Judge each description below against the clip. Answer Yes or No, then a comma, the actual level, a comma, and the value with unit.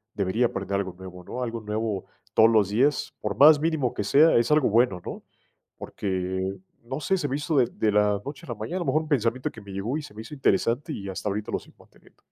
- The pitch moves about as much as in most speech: No, wide, 5.9 semitones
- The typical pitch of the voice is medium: No, low, 115 Hz